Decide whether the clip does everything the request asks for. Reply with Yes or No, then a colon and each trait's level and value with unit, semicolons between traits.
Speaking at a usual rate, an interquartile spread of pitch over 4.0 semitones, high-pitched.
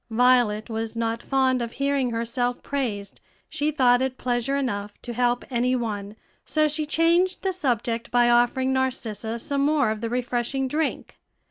No: average, 160 wpm; average, 2.9 semitones; high, 245 Hz